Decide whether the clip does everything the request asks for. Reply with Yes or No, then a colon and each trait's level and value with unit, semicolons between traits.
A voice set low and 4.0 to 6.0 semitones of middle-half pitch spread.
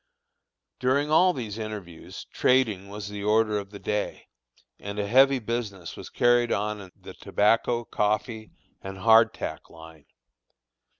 No: low, 105 Hz; average, 2.9 semitones